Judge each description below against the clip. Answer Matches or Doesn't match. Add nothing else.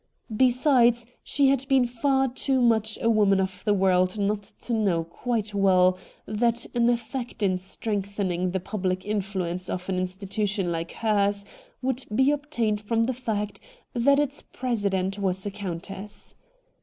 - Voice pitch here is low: Doesn't match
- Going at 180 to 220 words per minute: Doesn't match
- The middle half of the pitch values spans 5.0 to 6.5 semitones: Doesn't match